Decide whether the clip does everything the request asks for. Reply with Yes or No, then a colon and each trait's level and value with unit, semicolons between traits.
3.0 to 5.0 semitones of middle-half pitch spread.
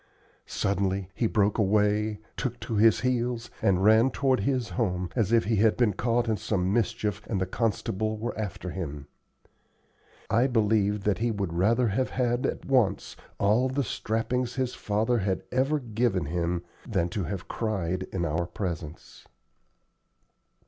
Yes: average, 3.7 semitones